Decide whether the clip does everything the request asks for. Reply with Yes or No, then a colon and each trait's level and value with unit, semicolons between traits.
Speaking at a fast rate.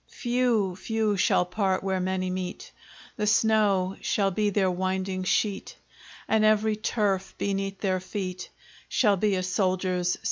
No: average, 145 wpm